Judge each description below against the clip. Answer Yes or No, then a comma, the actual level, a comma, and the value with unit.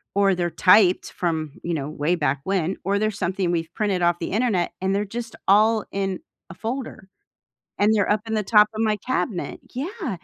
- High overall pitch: Yes, high, 195 Hz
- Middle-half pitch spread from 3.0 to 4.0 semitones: Yes, average, 3.6 semitones